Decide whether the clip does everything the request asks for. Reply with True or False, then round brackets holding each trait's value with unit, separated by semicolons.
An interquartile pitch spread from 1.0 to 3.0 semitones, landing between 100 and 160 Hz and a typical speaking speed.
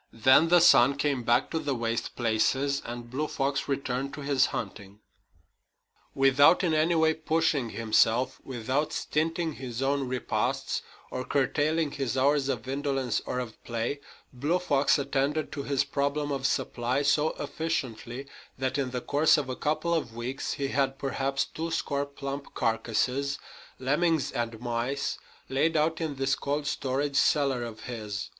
True (2.7 semitones; 135 Hz; 155 wpm)